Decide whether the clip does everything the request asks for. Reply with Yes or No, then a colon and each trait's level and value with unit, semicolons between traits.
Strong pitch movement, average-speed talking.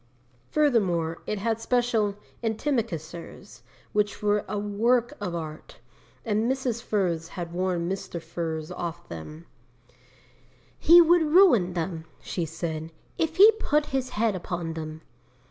No: wide, 6.1 semitones; slow, 130 wpm